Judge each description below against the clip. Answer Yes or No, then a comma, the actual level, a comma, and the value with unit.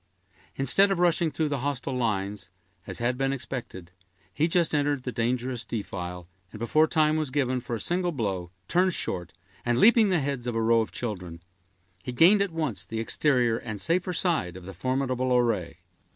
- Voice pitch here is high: No, low, 125 Hz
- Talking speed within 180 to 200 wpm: Yes, average, 185 wpm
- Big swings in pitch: Yes, wide, 5.7 semitones